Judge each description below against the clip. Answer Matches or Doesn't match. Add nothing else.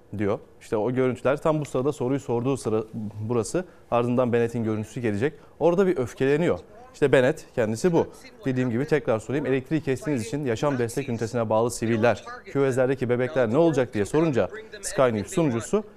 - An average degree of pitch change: Matches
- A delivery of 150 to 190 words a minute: Matches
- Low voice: Matches